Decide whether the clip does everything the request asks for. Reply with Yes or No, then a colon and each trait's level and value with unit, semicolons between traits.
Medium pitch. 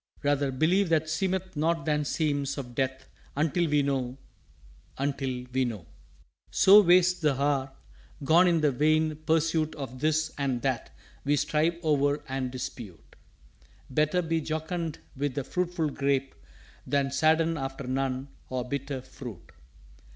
Yes: medium, 145 Hz